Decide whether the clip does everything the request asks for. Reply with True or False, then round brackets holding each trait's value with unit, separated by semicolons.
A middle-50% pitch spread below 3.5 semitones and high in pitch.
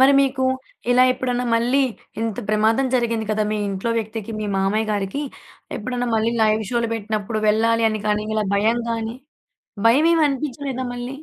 True (2.8 semitones; 230 Hz)